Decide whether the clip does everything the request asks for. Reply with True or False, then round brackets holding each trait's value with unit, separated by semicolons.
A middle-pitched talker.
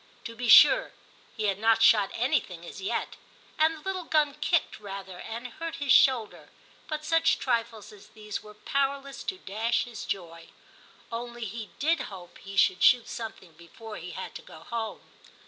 False (230 Hz)